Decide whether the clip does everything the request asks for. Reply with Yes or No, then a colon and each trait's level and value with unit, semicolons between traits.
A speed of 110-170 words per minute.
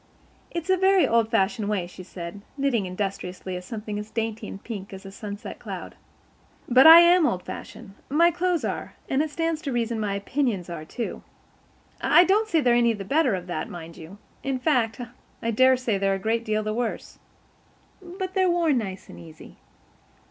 No: average, 190 wpm